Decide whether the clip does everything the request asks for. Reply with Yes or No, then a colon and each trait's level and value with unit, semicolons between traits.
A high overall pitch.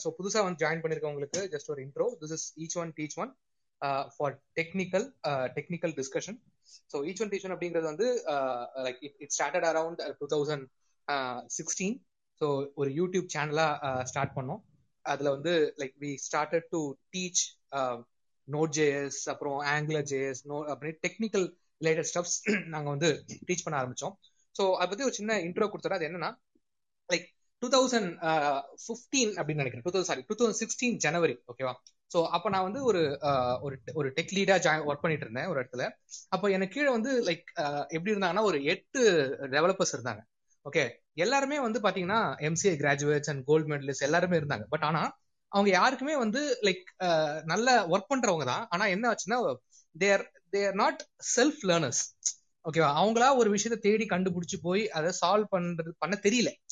No: medium, 170 Hz